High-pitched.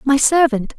Yes: very high, 270 Hz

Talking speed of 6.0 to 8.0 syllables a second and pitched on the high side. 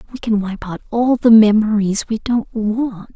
No: 4.4 syllables/s; high, 220 Hz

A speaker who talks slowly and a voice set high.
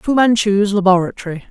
Yes: slow, 120 wpm; high, 200 Hz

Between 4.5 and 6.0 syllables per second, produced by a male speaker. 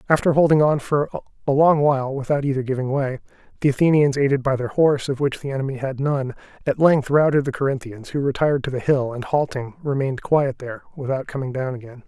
No: 6.3 syllables/s; male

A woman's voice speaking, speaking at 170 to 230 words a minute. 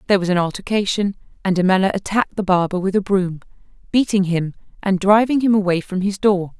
Yes: female; average, 190 wpm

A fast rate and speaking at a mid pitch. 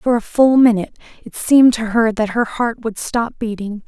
No: fast, 215 wpm; high, 225 Hz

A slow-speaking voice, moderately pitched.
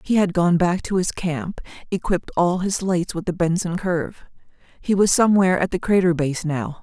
No: average, 200 wpm; medium, 180 Hz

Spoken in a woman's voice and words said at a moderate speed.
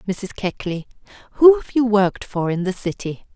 Yes: female; average, 180 wpm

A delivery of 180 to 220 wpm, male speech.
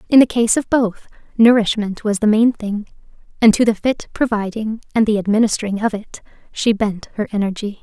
No: average, 185 wpm; female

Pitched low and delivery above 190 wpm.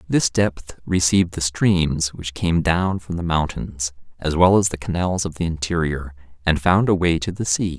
Yes: very low, 85 Hz; average, 200 wpm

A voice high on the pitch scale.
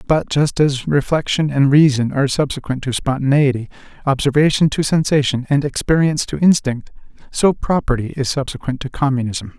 No: medium, 140 Hz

